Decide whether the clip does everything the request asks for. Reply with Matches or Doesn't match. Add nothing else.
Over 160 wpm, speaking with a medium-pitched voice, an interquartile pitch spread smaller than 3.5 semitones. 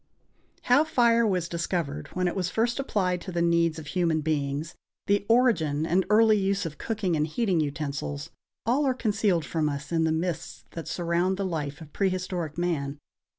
Doesn't match